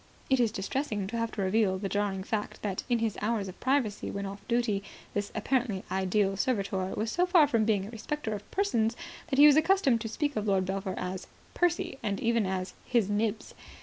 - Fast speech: Yes, fast, 210 wpm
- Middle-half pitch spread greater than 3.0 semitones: Yes, average, 3.7 semitones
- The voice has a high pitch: Yes, high, 215 Hz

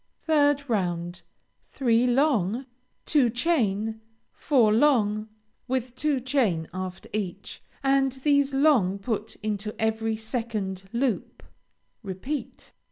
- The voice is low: No, high, 230 Hz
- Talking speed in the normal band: No, slow, 100 wpm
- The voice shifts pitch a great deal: No, average, 4.8 semitones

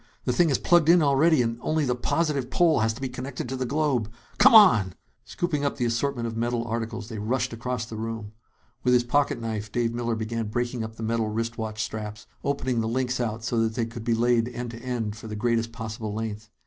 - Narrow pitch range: Yes, narrow, 2.3 semitones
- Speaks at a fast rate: Yes, fast, 230 wpm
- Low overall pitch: Yes, low, 115 Hz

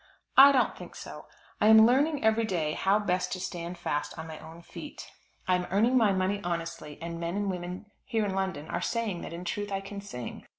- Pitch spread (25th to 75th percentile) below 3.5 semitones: No, average, 3.8 semitones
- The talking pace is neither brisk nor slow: No, fast, 220 wpm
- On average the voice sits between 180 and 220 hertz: Yes, high, 190 Hz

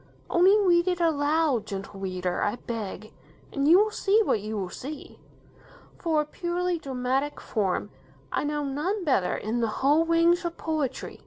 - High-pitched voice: Yes, very high, 295 Hz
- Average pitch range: No, wide, 7.2 semitones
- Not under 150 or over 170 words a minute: Yes, average, 165 wpm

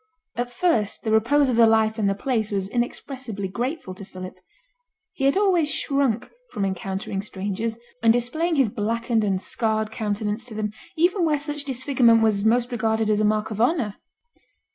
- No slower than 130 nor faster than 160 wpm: No, average, 175 wpm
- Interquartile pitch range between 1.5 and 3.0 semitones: No, average, 3.7 semitones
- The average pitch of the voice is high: Yes, high, 225 Hz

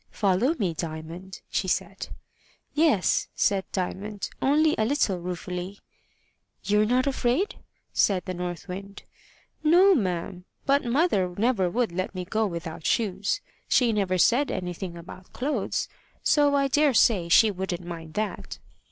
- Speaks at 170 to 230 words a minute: No, average, 140 wpm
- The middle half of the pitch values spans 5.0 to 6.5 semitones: Yes, wide, 5.6 semitones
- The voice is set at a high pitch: Yes, high, 195 Hz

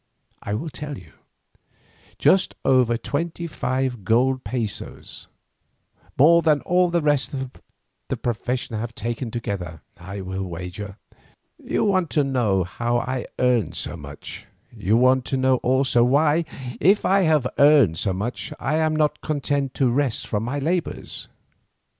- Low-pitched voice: Yes, low, 130 Hz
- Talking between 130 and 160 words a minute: Yes, average, 145 wpm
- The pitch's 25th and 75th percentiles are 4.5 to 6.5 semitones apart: Yes, average, 5.2 semitones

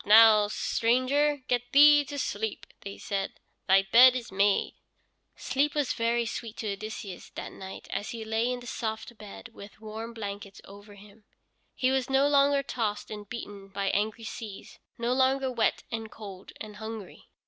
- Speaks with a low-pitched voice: No, high, 225 Hz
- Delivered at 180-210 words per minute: No, average, 170 wpm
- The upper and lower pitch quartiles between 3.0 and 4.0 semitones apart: Yes, average, 3.5 semitones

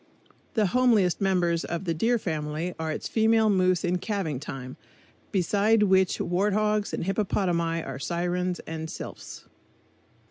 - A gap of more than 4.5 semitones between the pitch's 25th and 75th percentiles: No, average, 3.8 semitones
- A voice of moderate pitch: Yes, medium, 180 Hz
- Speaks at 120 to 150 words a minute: Yes, slow, 135 wpm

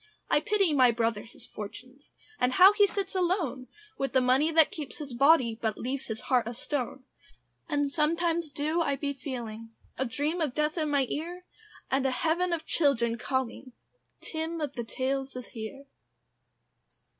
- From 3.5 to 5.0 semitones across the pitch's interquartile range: Yes, average, 4.2 semitones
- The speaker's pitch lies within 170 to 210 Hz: No, very high, 275 Hz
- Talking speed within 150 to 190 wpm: Yes, average, 170 wpm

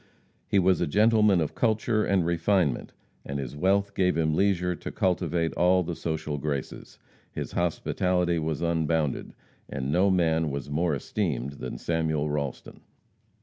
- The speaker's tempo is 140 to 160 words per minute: Yes, average, 145 wpm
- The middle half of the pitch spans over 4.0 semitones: No, average, 3.6 semitones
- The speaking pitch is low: Yes, very low, 85 Hz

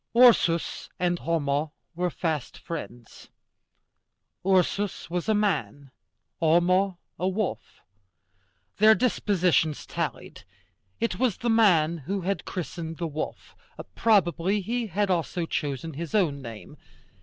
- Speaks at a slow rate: Yes, slow, 115 wpm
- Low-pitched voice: No, medium, 175 Hz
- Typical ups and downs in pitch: Yes, average, 3.9 semitones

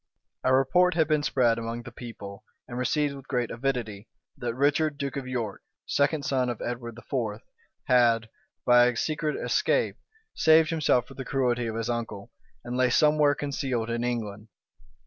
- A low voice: Yes, low, 125 Hz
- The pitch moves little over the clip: No, average, 3.3 semitones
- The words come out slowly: No, average, 165 wpm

